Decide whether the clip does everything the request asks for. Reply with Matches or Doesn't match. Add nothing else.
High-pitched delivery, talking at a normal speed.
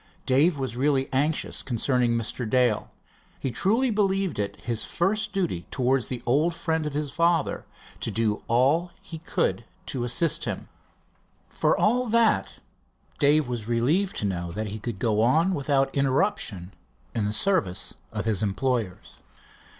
Doesn't match